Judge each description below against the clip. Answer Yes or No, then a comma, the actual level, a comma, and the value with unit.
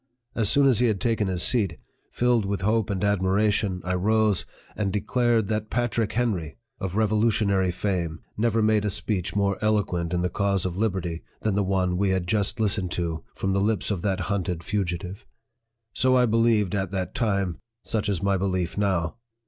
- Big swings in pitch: No, average, 2.9 semitones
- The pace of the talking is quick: No, average, 190 wpm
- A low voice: Yes, low, 100 Hz